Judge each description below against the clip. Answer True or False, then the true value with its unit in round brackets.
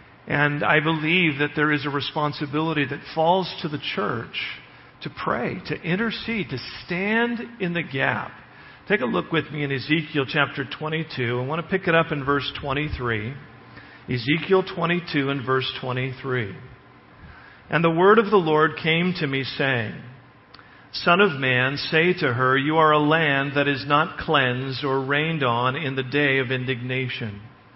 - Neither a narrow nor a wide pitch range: True (3.6 semitones)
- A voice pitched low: False (145 Hz)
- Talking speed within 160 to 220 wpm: True (165 wpm)